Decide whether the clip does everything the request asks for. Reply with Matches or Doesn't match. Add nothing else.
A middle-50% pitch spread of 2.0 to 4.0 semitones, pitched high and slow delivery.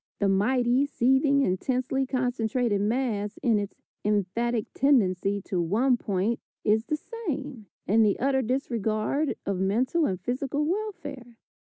Doesn't match